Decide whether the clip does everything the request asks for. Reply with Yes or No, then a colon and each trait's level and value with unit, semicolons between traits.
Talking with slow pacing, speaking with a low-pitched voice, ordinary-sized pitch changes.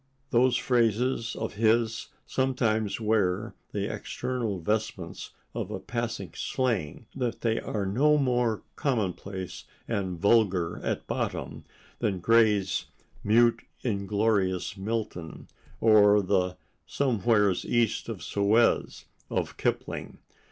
Yes: slow, 105 wpm; low, 110 Hz; average, 3.1 semitones